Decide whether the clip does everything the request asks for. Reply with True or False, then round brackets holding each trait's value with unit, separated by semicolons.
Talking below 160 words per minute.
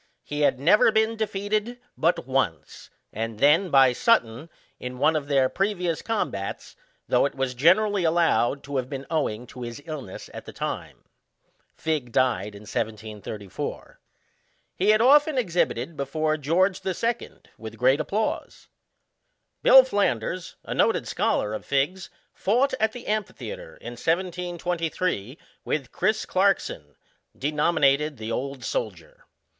True (140 wpm)